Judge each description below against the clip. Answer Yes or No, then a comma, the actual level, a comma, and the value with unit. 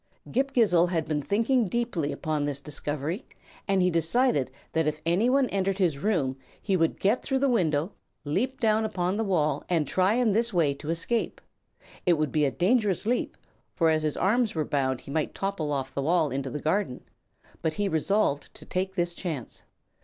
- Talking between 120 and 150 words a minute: No, average, 190 wpm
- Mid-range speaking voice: Yes, medium, 175 Hz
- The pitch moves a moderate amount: No, wide, 5.8 semitones